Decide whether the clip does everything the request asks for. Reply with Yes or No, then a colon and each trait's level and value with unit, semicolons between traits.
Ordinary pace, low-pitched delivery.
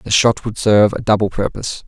No: fast, 225 wpm; low, 105 Hz